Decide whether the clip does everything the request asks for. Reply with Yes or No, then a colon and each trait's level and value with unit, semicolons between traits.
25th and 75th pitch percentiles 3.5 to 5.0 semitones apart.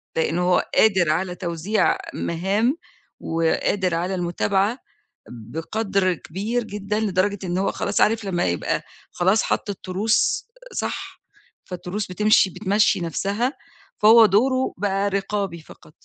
No: average, 3.1 semitones